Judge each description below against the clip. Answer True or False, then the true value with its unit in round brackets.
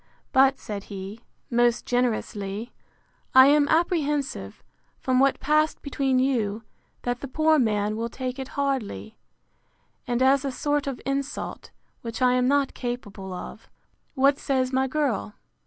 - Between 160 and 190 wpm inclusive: False (140 wpm)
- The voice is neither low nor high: False (260 Hz)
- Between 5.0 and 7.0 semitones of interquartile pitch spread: False (3.3 semitones)